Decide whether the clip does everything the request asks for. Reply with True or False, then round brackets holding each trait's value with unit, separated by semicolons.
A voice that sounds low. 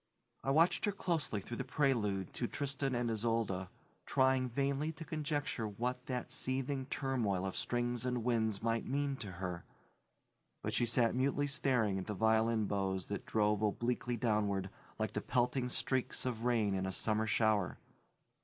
True (120 Hz)